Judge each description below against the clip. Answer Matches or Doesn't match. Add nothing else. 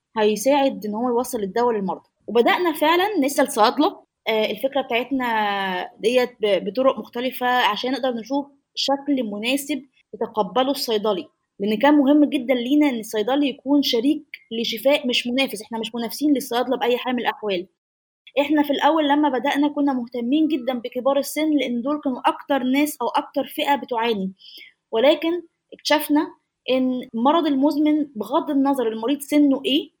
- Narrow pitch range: Doesn't match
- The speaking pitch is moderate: Doesn't match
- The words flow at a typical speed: Doesn't match